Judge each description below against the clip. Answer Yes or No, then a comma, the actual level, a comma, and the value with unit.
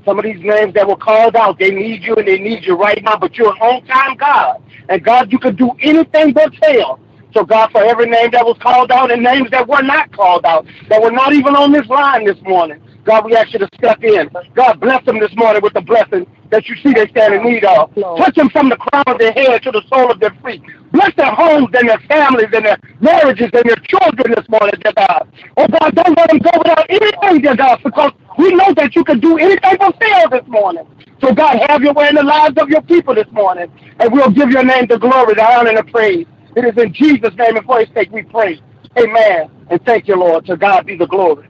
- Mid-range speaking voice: No, high, 245 Hz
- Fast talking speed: Yes, fast, 255 wpm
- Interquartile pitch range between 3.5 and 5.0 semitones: No, wide, 5.5 semitones